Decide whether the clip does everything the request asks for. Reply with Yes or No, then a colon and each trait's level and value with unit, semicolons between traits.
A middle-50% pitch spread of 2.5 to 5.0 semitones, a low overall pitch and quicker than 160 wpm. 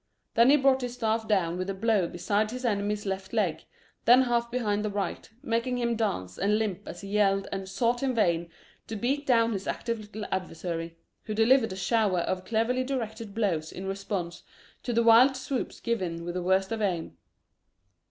No: average, 3.7 semitones; high, 210 Hz; average, 190 wpm